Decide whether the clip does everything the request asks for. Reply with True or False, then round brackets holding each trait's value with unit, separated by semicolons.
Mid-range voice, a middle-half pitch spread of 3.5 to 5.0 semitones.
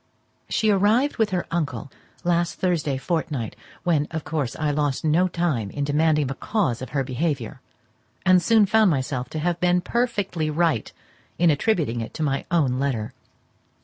True (160 Hz; 4.5 semitones)